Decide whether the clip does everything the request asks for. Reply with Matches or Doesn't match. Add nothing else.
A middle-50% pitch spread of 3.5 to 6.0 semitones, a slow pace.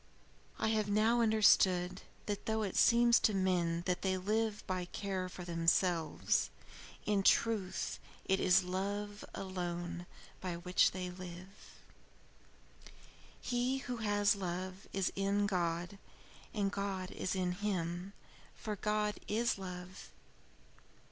Doesn't match